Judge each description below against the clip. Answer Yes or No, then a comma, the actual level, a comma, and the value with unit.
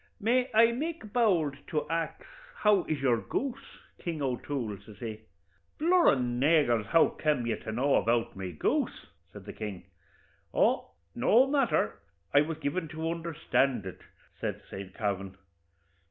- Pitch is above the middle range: No, medium, 145 Hz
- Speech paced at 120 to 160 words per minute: Yes, average, 150 wpm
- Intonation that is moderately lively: No, wide, 8.3 semitones